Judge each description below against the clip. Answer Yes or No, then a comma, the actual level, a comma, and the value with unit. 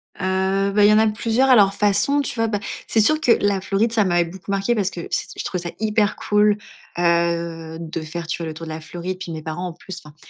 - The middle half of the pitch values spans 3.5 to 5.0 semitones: Yes, average, 3.8 semitones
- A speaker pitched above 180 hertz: Yes, high, 190 Hz